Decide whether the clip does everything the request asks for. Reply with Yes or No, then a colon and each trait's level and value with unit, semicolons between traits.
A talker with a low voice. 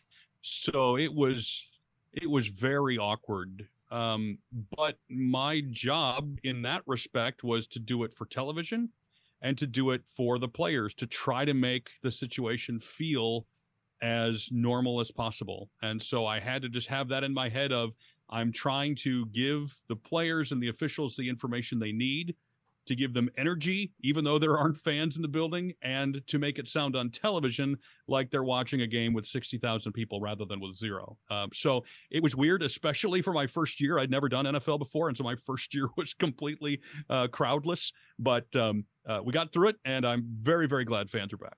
Yes: low, 130 Hz